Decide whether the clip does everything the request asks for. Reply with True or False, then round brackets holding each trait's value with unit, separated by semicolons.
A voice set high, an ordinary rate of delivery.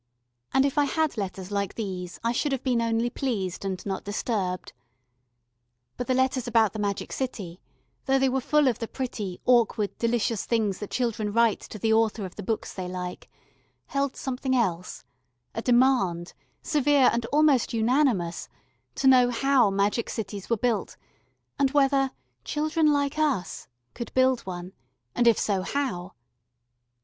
True (230 Hz; 160 wpm)